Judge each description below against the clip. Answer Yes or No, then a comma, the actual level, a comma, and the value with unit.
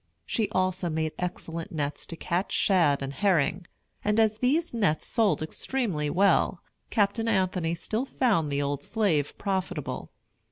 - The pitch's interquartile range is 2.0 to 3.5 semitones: No, average, 5.0 semitones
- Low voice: No, medium, 185 Hz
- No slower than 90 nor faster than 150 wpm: Yes, average, 145 wpm